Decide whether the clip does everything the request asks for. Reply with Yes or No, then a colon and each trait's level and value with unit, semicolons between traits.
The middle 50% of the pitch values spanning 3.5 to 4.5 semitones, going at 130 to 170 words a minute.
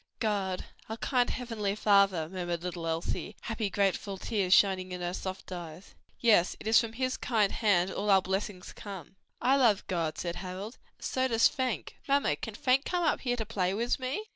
No: average, 4.0 semitones; average, 190 wpm